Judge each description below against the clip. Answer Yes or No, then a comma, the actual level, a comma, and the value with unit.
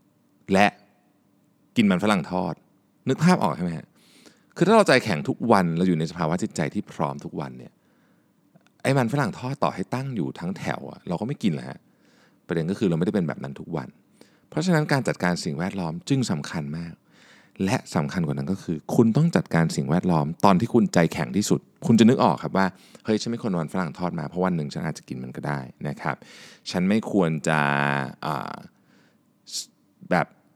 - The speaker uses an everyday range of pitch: No, wide, 8.3 semitones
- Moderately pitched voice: No, very low, 90 Hz